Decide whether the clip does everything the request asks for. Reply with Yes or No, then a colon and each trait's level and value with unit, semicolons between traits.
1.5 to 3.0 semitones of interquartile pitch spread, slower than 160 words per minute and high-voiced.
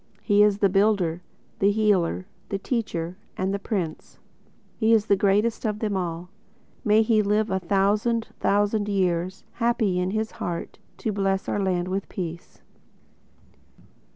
Yes: narrow, 2.5 semitones; average, 150 wpm; high, 200 Hz